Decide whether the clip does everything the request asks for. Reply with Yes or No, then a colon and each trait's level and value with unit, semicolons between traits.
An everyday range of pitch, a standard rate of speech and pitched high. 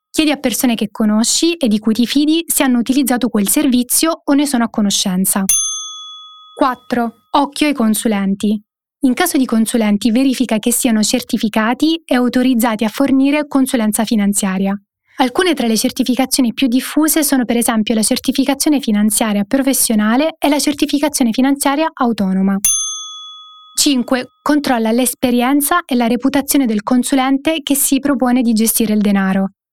Yes: average, 4.2 semitones; average, 145 wpm; very high, 255 Hz